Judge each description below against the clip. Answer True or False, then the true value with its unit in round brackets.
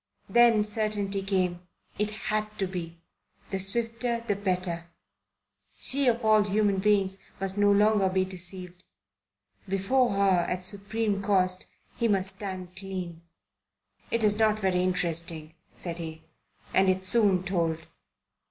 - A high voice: True (195 Hz)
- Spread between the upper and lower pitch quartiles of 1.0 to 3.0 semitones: True (2.5 semitones)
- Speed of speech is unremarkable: False (130 wpm)